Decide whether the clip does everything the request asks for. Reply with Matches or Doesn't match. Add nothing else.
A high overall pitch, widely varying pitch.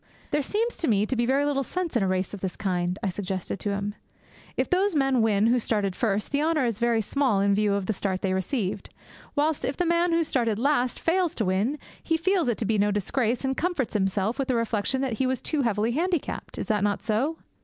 Matches